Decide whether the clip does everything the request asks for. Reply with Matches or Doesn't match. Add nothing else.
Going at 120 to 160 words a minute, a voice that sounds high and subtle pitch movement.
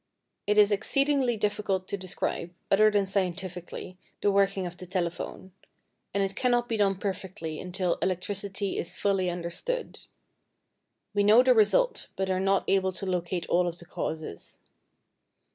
Matches